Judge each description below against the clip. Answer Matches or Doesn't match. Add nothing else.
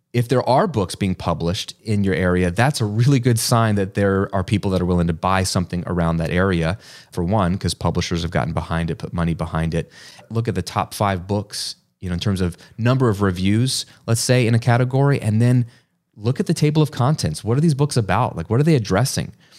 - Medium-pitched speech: Doesn't match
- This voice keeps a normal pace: Doesn't match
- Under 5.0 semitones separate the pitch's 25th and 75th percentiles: Doesn't match